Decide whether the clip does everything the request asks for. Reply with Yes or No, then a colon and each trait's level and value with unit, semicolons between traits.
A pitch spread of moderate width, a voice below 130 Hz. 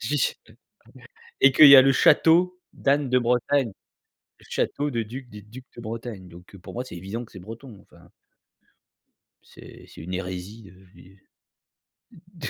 No: wide, 5.8 semitones; low, 120 Hz